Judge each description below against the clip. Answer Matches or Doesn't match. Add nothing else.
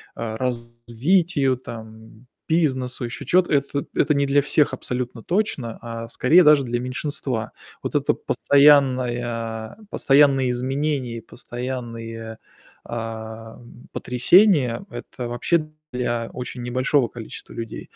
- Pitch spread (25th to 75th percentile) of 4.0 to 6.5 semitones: Doesn't match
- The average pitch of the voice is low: Matches